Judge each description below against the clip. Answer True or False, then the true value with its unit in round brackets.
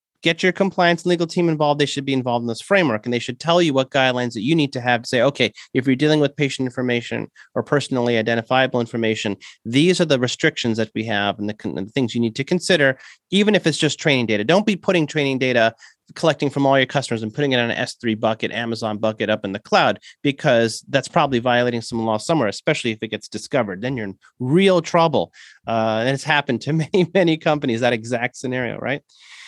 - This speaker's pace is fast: True (230 wpm)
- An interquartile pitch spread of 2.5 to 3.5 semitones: False (4.7 semitones)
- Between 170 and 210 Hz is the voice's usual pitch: False (130 Hz)